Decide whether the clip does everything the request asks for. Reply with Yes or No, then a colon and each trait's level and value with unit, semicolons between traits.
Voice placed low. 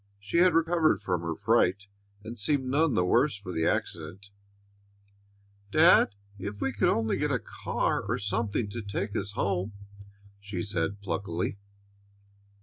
Yes: low, 100 Hz